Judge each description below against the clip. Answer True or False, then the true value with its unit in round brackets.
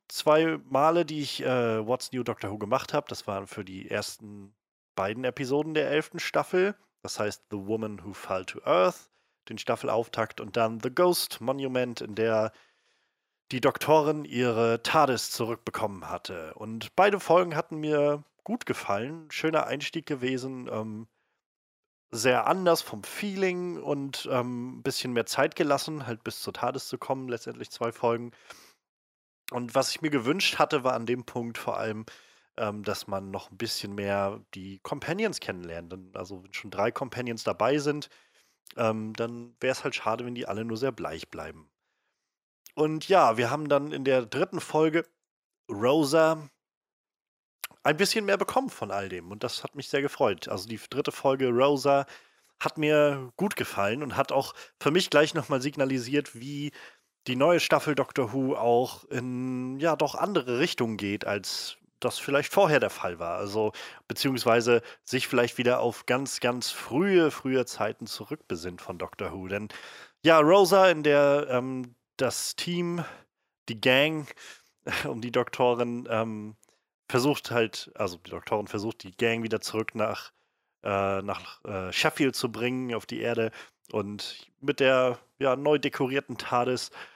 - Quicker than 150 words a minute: True (160 wpm)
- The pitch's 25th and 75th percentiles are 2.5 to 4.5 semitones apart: False (4.9 semitones)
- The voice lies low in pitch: True (125 Hz)